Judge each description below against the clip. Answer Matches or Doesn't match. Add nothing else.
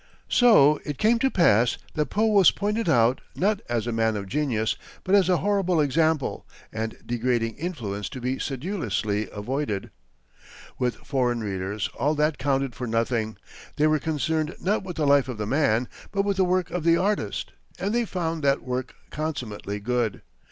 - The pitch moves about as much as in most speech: Doesn't match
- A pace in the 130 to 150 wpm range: Doesn't match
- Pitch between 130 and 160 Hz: Matches